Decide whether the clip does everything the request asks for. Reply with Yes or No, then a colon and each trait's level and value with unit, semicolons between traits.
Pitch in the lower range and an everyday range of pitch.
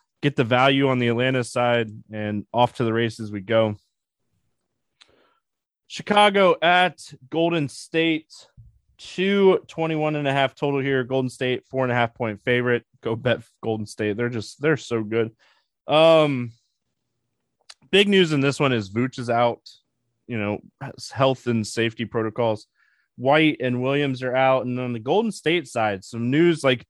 Yes: low, 125 Hz; average, 4.4 semitones